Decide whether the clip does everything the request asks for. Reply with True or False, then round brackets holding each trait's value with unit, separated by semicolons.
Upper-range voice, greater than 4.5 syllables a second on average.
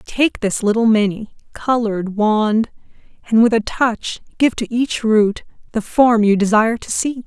False (225 Hz; 4.4 syllables/s)